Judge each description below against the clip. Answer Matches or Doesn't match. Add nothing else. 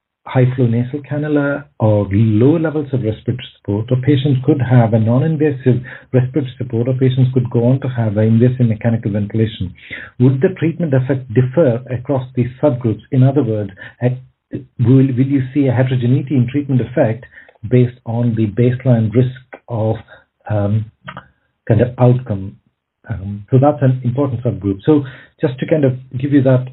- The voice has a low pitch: Matches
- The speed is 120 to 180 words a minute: Matches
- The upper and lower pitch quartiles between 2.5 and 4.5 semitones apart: Matches